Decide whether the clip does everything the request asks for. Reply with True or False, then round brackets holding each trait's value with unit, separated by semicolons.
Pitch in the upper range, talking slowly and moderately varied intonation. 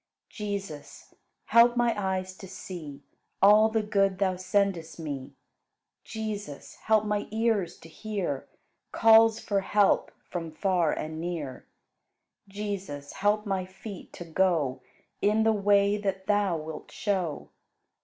True (195 Hz; 130 wpm; 3.6 semitones)